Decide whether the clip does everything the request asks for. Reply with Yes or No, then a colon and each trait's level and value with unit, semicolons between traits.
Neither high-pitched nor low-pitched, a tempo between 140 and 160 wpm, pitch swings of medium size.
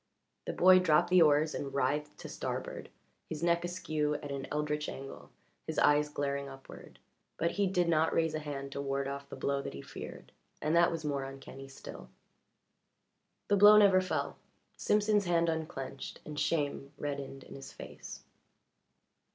No: medium, 150 Hz; average, 170 wpm; average, 3.4 semitones